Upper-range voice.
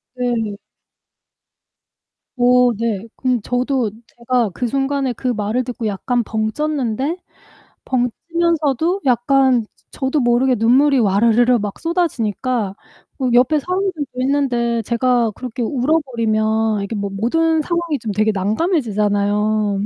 Yes: high, 245 Hz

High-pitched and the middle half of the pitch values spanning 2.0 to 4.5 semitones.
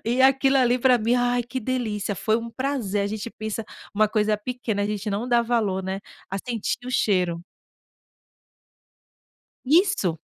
Yes: high, 230 Hz; average, 3.4 semitones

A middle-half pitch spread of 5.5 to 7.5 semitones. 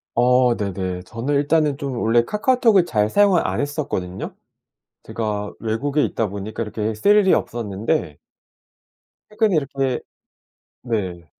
Yes: wide, 6.1 semitones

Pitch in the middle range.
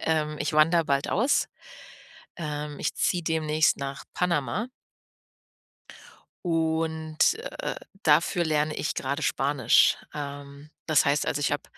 Yes: medium, 155 Hz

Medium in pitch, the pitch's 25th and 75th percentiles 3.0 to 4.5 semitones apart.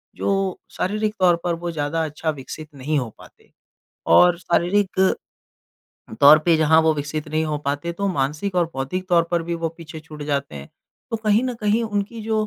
Yes: medium, 165 Hz; average, 3.8 semitones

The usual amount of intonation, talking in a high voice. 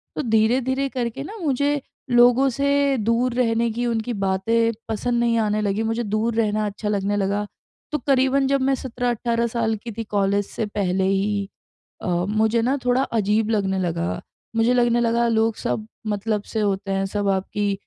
Yes: average, 3.0 semitones; high, 225 Hz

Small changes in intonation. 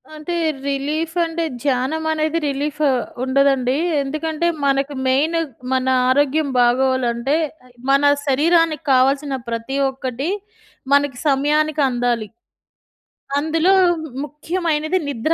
No: average, 3.0 semitones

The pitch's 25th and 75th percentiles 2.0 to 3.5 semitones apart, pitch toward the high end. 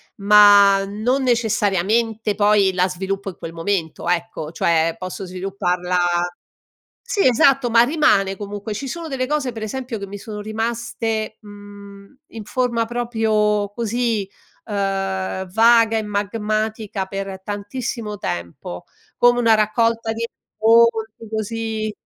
Yes: average, 2.7 semitones; high, 210 Hz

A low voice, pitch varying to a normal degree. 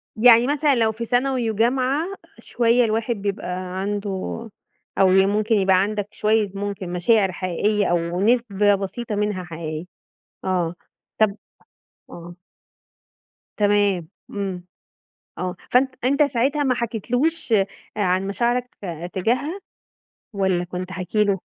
No: high, 205 Hz; average, 4.0 semitones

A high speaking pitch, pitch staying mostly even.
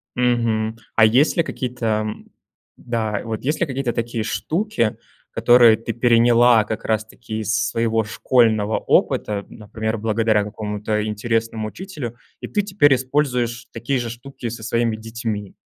No: low, 115 Hz; narrow, 2.0 semitones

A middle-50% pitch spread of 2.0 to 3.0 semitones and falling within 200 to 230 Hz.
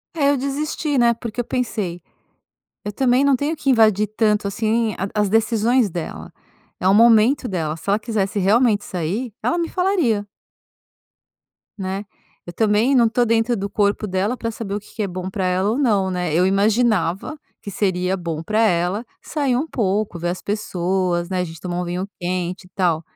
No: average, 4.3 semitones; high, 210 Hz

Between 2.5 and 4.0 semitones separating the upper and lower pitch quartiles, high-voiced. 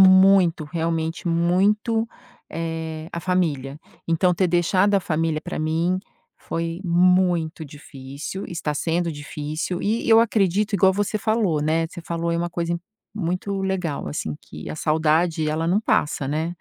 No: average, 2.9 semitones; medium, 170 Hz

